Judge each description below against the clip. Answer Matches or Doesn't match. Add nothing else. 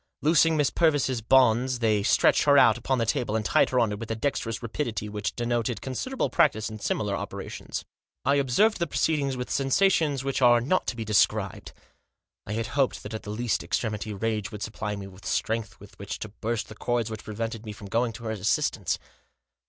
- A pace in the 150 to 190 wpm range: Doesn't match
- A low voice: Matches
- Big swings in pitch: Doesn't match